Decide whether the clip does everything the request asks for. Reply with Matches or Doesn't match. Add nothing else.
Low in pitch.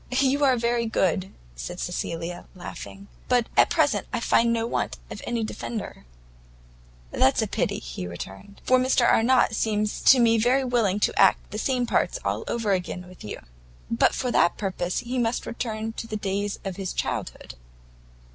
Doesn't match